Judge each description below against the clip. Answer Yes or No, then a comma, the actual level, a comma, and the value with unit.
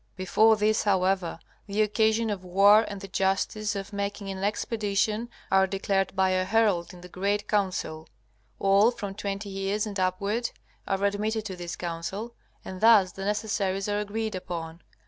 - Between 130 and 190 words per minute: Yes, average, 165 wpm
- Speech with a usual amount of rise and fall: No, narrow, 2.0 semitones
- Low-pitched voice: No, high, 200 Hz